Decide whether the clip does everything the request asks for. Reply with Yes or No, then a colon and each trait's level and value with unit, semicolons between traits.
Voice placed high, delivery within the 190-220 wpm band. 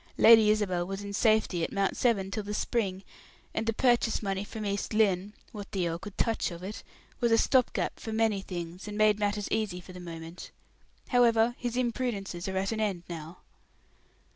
Yes: high, 205 Hz; average, 195 wpm